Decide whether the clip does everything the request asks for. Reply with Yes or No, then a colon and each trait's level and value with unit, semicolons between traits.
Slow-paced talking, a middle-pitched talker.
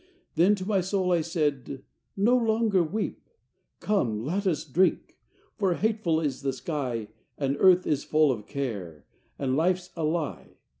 No: average, 160 wpm; medium, 165 Hz